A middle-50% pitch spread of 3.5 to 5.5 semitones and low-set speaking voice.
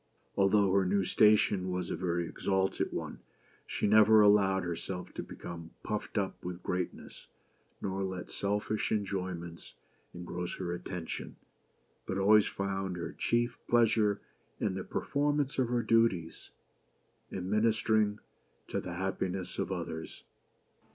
No: average, 2.9 semitones; very low, 95 Hz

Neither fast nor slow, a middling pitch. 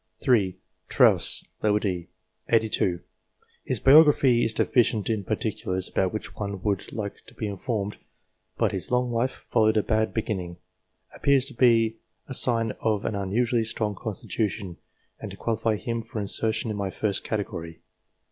No: average, 155 wpm; low, 110 Hz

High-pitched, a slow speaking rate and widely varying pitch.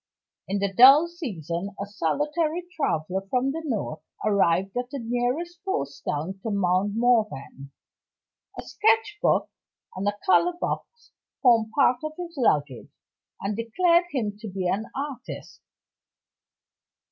Yes: high, 230 Hz; slow, 130 wpm; wide, 7.8 semitones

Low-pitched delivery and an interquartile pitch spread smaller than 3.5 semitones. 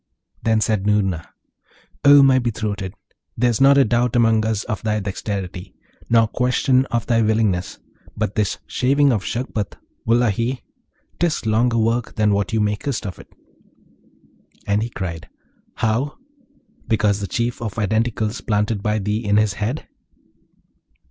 Yes: low, 110 Hz; narrow, 2.6 semitones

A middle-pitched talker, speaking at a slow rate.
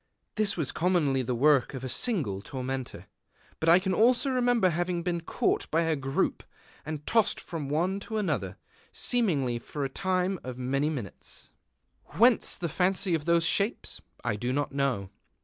No: medium, 160 Hz; average, 170 wpm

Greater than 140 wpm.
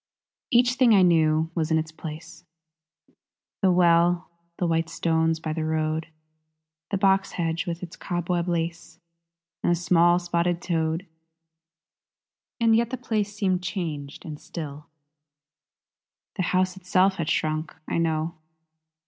No: slow, 135 wpm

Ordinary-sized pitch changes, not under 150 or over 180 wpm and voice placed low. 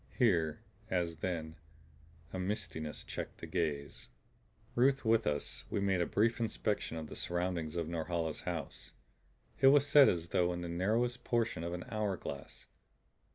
Yes: average, 4.9 semitones; average, 155 wpm; very low, 90 Hz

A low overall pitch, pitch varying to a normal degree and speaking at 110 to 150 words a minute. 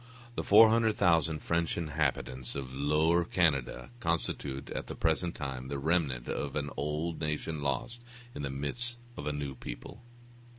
Yes: very low, 75 Hz; average, 3.5 semitones; average, 145 wpm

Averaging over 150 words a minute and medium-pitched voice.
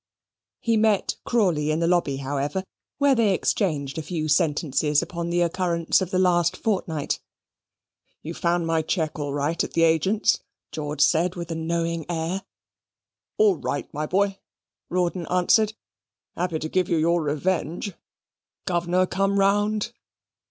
No: average, 145 wpm; medium, 170 Hz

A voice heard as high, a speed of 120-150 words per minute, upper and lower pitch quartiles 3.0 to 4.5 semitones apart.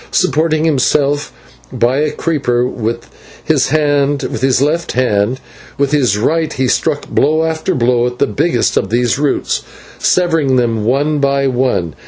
No: medium, 140 Hz; average, 140 wpm; average, 3.8 semitones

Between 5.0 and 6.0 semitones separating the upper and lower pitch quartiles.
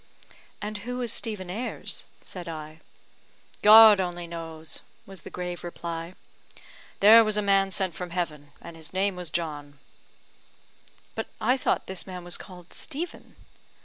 No: average, 3.6 semitones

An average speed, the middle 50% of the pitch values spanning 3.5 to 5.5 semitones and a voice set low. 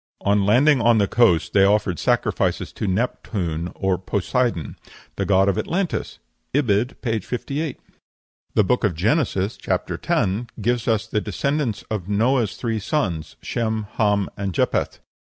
Yes: average, 145 wpm; average, 4.0 semitones; low, 105 Hz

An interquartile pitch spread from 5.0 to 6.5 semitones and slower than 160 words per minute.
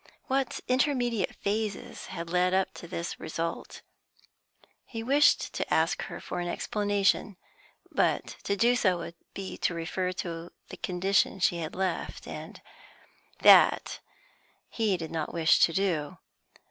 No: average, 3.8 semitones; average, 140 wpm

